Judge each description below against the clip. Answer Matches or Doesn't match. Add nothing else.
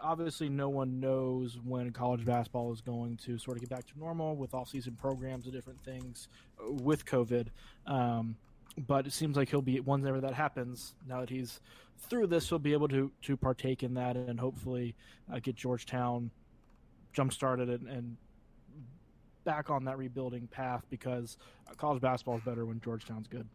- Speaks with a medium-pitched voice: Doesn't match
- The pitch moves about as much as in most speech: Doesn't match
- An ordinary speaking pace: Matches